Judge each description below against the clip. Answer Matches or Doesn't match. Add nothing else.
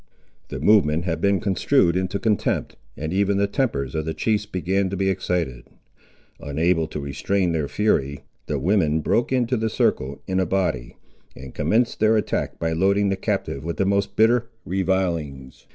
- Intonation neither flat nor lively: Matches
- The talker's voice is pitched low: Matches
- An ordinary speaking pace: Matches